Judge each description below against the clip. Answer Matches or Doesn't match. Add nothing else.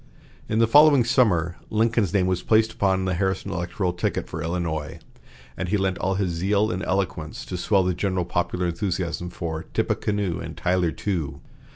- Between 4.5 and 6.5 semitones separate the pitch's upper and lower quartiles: Doesn't match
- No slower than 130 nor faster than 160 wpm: Doesn't match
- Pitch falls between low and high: Doesn't match